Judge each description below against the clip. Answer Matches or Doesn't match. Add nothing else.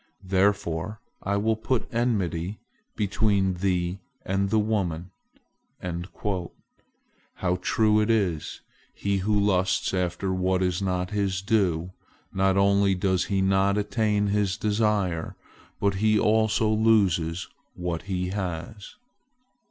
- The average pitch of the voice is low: Matches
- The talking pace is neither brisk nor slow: Doesn't match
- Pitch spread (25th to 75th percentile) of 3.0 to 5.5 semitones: Doesn't match